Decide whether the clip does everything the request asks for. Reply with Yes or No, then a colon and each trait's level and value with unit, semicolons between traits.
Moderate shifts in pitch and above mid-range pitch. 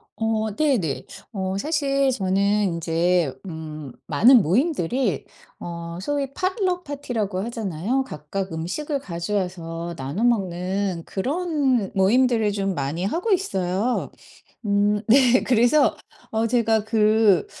No: wide, 6.3 semitones; high, 210 Hz